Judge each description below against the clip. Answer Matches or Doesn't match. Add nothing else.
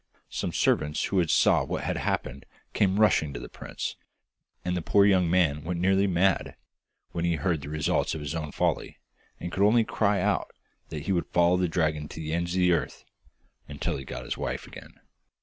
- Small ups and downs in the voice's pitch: Doesn't match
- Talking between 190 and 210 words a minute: Matches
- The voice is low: Matches